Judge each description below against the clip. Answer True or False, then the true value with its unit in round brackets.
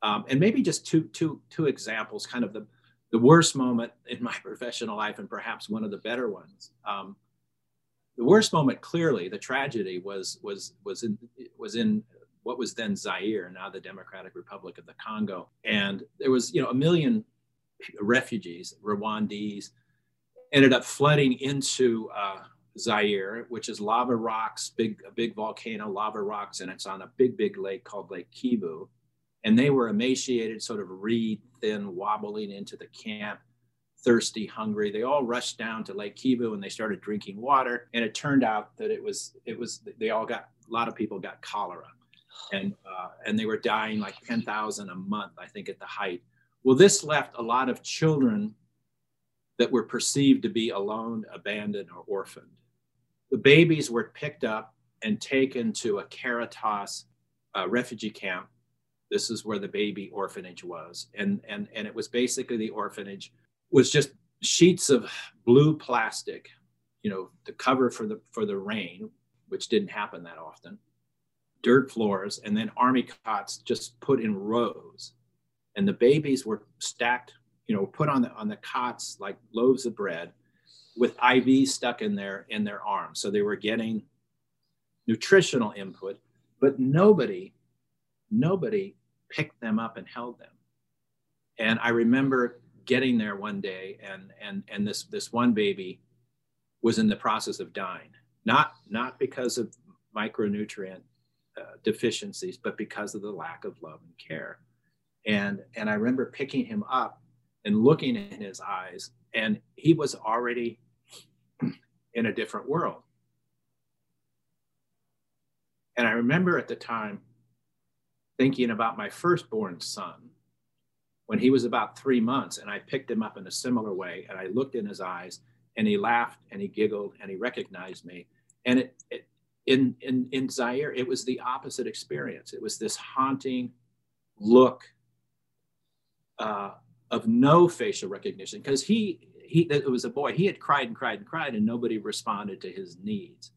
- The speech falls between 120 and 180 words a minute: True (165 wpm)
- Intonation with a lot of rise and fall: True (8.7 semitones)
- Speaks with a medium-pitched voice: False (120 Hz)